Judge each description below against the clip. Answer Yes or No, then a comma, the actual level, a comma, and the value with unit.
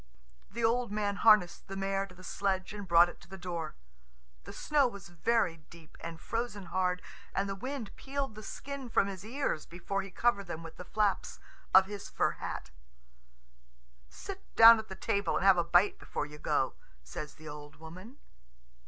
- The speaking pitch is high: Yes, high, 195 Hz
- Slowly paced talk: No, average, 190 wpm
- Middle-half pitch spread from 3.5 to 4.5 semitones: Yes, average, 4.2 semitones